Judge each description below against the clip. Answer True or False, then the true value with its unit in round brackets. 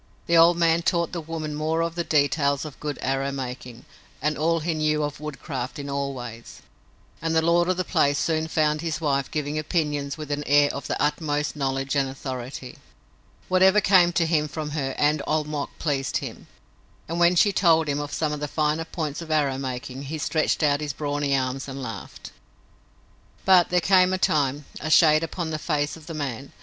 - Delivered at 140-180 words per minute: False (205 wpm)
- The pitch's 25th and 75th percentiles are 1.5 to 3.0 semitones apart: True (2.6 semitones)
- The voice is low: False (150 Hz)